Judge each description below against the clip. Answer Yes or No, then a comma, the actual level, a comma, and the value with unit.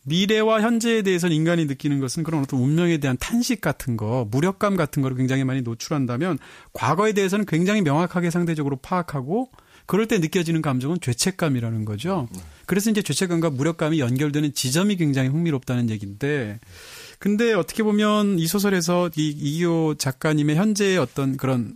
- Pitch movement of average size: No, wide, 6.0 semitones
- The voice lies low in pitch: No, medium, 160 Hz